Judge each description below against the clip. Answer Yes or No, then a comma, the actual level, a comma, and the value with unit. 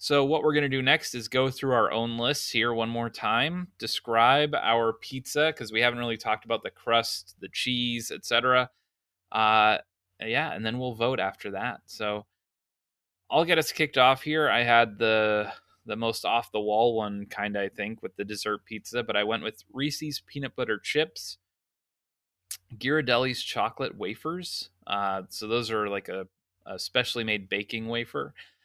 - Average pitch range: Yes, average, 3.5 semitones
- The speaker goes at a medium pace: Yes, average, 175 wpm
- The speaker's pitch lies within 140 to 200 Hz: No, low, 115 Hz